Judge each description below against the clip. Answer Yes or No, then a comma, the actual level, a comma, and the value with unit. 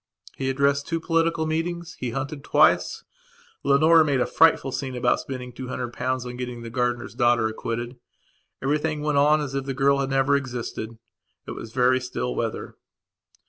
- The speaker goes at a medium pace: Yes, average, 180 wpm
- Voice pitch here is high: No, low, 135 Hz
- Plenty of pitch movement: No, average, 3.2 semitones